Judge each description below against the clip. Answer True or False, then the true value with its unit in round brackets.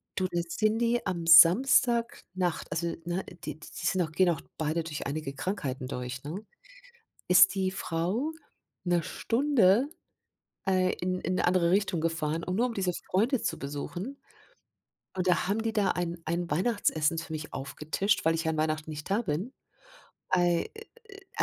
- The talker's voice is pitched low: False (175 Hz)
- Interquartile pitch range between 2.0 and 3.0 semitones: False (3.8 semitones)